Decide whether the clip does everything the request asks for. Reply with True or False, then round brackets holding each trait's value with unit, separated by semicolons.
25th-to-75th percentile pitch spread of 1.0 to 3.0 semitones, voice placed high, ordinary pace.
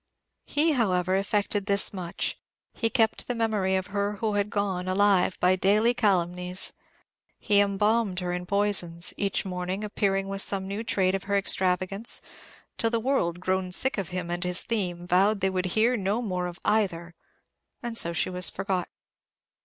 True (2.5 semitones; 195 Hz; 170 wpm)